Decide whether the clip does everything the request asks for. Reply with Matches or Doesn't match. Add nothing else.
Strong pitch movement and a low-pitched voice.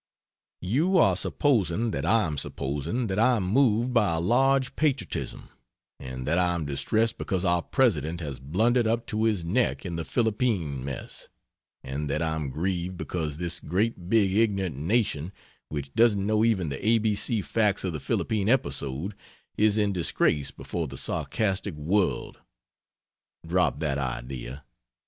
Matches